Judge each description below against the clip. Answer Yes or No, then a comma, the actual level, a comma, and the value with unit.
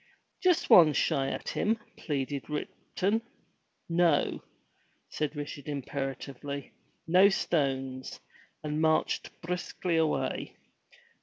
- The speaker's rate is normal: No, slow, 90 wpm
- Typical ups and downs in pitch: Yes, average, 3.7 semitones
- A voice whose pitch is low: No, medium, 150 Hz